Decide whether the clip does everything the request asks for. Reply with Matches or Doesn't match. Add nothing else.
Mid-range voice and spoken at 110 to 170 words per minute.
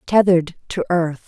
Matches